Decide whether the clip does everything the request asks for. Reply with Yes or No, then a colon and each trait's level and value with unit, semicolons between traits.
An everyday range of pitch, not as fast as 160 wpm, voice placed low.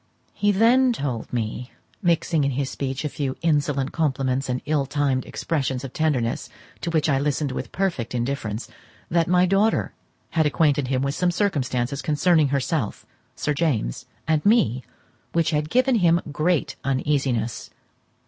No: average, 4.1 semitones; average, 150 wpm; medium, 145 Hz